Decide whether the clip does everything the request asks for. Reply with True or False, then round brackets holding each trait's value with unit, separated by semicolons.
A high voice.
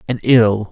False (115 Hz)